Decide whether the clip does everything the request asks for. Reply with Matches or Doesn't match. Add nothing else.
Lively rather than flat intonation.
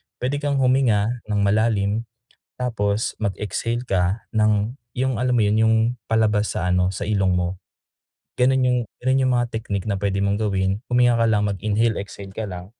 Doesn't match